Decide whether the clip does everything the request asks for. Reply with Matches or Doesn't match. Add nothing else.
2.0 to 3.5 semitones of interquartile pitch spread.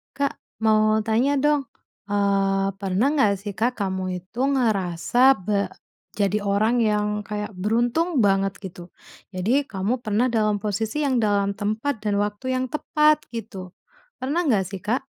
Doesn't match